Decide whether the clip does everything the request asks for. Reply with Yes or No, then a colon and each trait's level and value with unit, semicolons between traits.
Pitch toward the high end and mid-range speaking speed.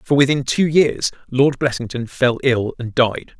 No: low, 130 Hz; average, 175 wpm